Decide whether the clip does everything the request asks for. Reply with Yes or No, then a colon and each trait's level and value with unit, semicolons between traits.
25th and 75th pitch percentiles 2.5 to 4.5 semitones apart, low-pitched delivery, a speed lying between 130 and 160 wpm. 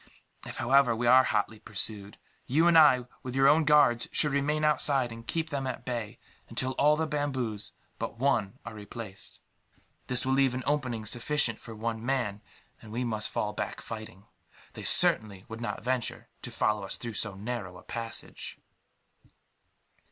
No: average, 3.9 semitones; low, 120 Hz; average, 170 wpm